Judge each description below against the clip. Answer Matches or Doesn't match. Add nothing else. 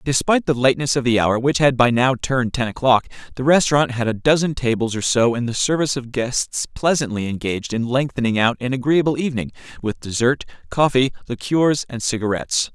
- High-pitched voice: Doesn't match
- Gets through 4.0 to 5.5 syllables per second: Doesn't match